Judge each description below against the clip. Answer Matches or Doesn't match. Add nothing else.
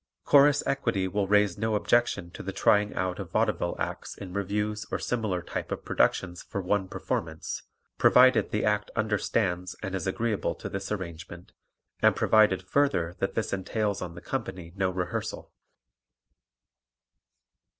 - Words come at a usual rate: Matches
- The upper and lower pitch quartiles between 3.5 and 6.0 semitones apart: Doesn't match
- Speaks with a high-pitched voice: Doesn't match